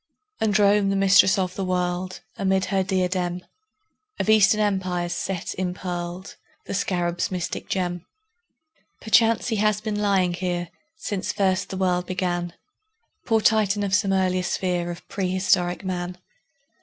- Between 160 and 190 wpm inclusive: No, average, 140 wpm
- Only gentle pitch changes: Yes, narrow, 2.0 semitones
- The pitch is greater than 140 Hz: Yes, medium, 185 Hz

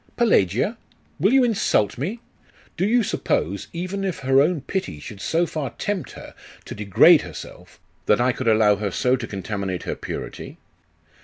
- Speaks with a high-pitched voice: No, low, 135 Hz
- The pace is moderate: Yes, average, 165 wpm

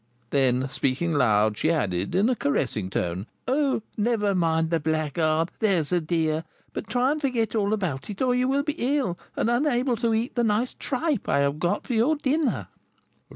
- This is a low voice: No, high, 195 Hz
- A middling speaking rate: Yes, average, 190 wpm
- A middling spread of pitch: No, wide, 8.4 semitones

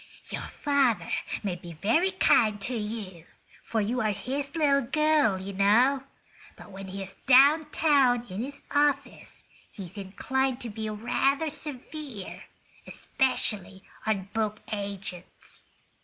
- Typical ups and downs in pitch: No, wide, 5.8 semitones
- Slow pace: Yes, slow, 125 wpm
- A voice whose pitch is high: Yes, high, 230 Hz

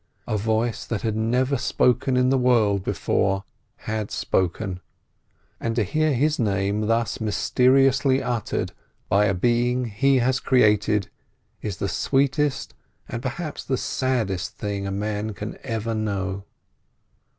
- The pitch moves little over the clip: No, average, 3.8 semitones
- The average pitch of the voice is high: No, low, 115 Hz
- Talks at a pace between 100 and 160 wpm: Yes, slow, 135 wpm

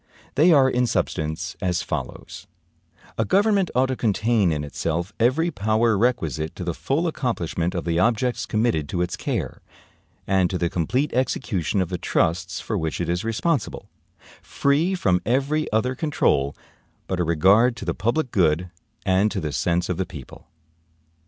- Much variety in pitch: Yes, wide, 6.6 semitones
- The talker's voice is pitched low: Yes, low, 100 Hz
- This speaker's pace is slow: No, average, 165 wpm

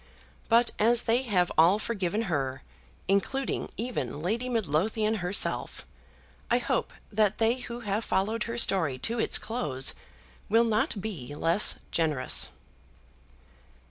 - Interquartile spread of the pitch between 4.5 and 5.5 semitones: Yes, average, 5.0 semitones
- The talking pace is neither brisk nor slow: No, slow, 125 wpm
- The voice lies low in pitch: No, high, 210 Hz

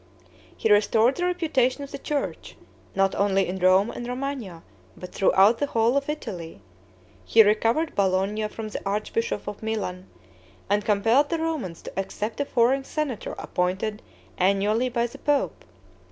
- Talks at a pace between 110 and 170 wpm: Yes, average, 155 wpm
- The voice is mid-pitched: No, high, 220 Hz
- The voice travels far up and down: Yes, wide, 5.7 semitones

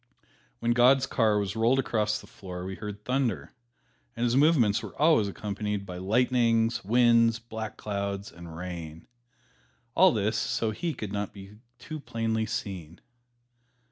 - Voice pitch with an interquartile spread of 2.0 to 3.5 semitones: Yes, average, 3.1 semitones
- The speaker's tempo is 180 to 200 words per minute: No, average, 145 wpm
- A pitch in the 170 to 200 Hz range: No, low, 110 Hz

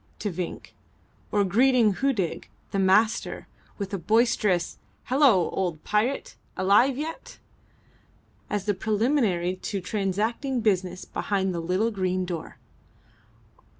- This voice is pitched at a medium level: No, high, 200 Hz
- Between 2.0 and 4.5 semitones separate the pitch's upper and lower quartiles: Yes, average, 3.7 semitones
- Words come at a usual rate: No, slow, 115 wpm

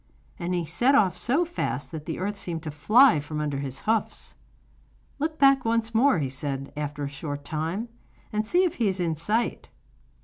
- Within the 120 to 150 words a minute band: No, average, 195 wpm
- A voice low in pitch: No, medium, 180 Hz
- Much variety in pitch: Yes, wide, 7.6 semitones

